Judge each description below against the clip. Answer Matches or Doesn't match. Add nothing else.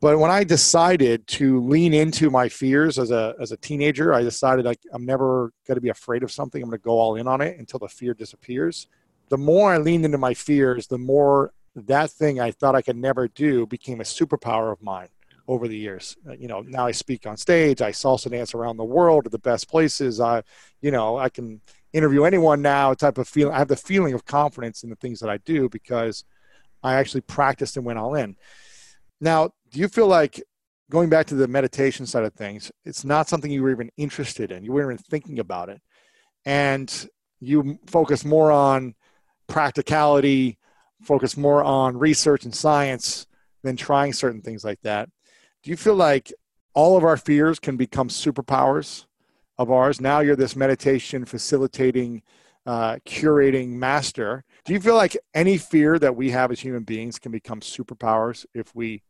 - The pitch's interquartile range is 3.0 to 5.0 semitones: Matches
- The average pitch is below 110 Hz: Doesn't match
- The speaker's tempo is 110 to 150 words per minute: Doesn't match